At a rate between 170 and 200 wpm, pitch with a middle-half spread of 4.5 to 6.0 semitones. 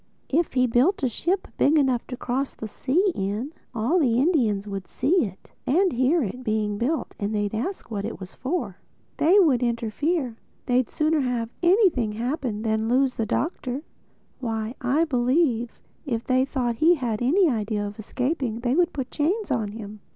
Yes: average, 180 wpm; wide, 5.4 semitones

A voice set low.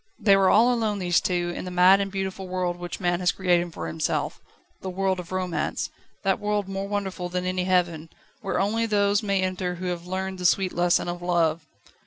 No: medium, 185 Hz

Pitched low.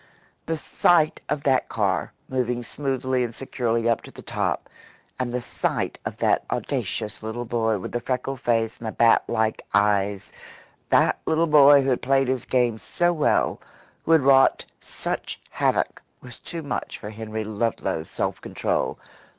Yes: low, 120 Hz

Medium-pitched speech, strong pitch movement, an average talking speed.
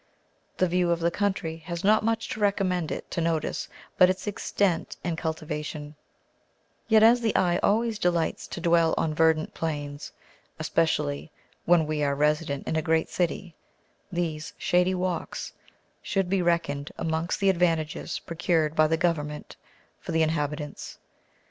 No: medium, 165 Hz; narrow, 2.6 semitones; average, 150 wpm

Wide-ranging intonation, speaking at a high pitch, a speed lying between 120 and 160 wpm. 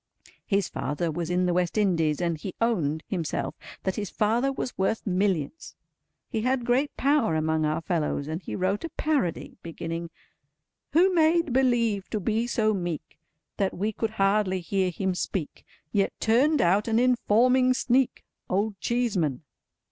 Yes: wide, 5.7 semitones; high, 200 Hz; average, 155 wpm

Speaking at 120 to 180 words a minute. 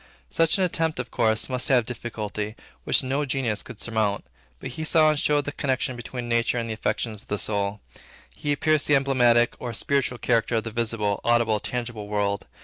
No: average, 195 wpm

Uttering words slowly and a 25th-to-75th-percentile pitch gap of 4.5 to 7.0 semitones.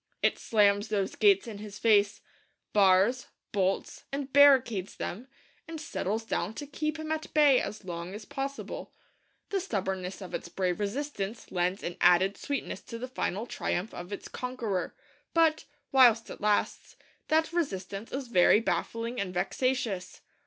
No: average, 150 wpm; wide, 5.5 semitones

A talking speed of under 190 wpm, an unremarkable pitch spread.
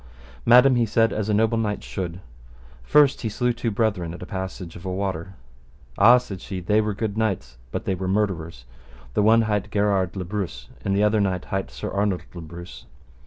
No: fast, 205 wpm; average, 3.0 semitones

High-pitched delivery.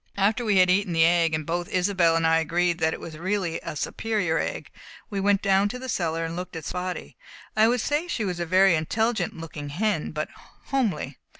No: medium, 180 Hz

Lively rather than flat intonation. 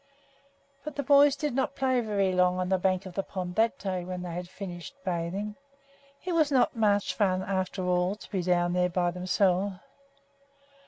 No: average, 3.4 semitones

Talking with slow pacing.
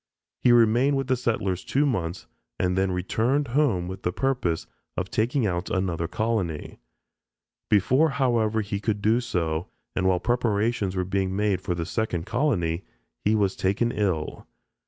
No: average, 155 wpm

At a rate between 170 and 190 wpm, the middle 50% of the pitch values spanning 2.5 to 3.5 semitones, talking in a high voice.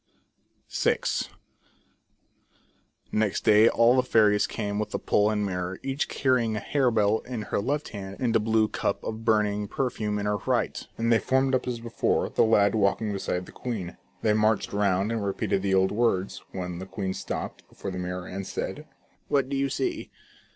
No: average, 185 wpm; average, 2.8 semitones; low, 105 Hz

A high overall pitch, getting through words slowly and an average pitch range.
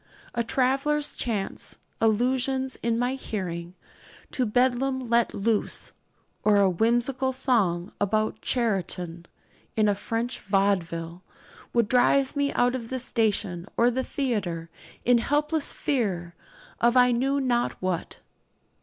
Yes: high, 235 Hz; slow, 125 wpm; average, 4.7 semitones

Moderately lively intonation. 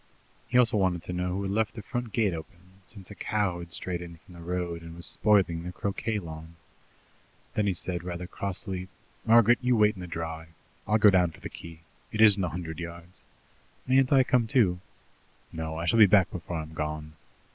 Yes: average, 3.8 semitones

